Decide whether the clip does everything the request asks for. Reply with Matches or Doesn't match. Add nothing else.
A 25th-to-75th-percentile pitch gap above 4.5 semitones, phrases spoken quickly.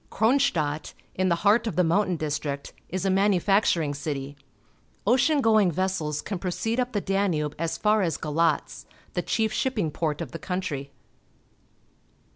Doesn't match